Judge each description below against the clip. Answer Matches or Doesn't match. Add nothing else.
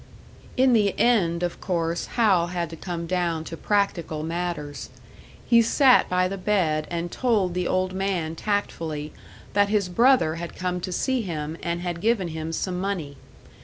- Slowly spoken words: Doesn't match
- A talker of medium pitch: Matches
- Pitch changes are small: Doesn't match